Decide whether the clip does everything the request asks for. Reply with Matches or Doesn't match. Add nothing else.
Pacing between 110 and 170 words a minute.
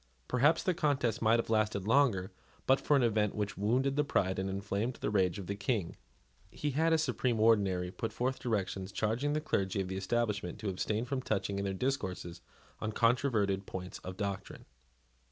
Doesn't match